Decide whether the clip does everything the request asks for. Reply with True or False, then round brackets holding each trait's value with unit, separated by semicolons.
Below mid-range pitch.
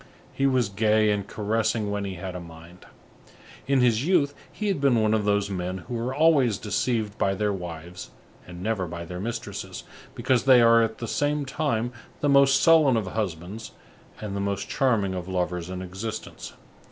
True (110 Hz)